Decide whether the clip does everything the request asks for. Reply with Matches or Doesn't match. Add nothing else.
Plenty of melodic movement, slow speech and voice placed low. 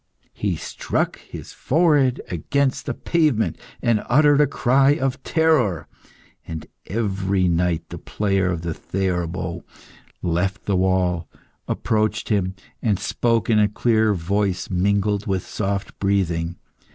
Doesn't match